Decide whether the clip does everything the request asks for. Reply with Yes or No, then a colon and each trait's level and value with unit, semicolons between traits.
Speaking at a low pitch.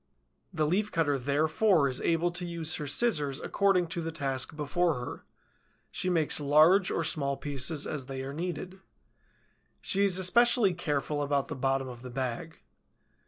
No: medium, 155 Hz